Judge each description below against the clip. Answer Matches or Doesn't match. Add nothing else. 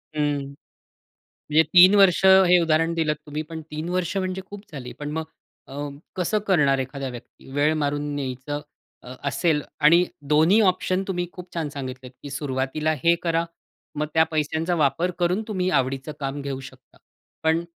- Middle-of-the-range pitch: Matches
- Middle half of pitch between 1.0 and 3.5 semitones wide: Doesn't match